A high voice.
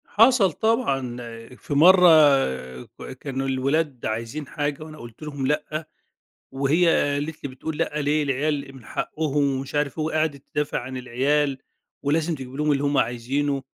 No: medium, 145 Hz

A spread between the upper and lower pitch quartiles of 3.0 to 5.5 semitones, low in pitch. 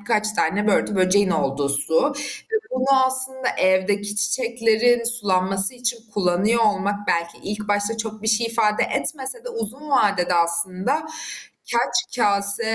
No: average, 3.8 semitones; high, 210 Hz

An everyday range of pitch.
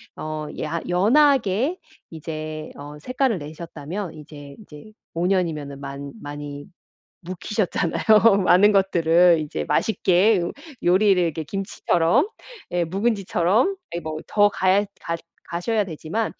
Yes: average, 4.8 semitones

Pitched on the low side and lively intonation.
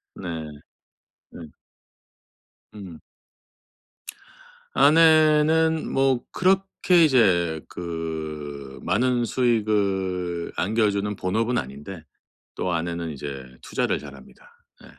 Yes: very low, 95 Hz; wide, 7.8 semitones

